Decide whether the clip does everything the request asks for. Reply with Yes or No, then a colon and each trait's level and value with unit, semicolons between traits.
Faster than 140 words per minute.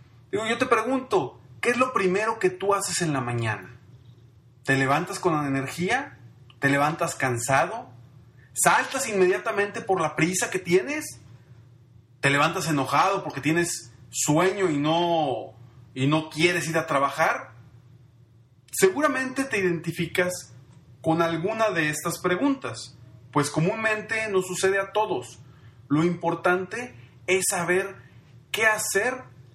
No: slow, 125 wpm